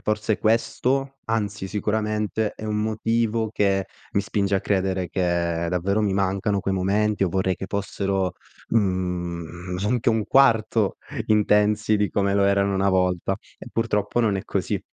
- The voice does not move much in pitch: Yes, narrow, 2.1 semitones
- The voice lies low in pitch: Yes, low, 100 Hz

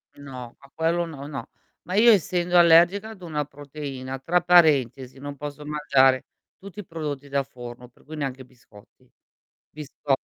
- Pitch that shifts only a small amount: No, average, 4.0 semitones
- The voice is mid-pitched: Yes, medium, 145 Hz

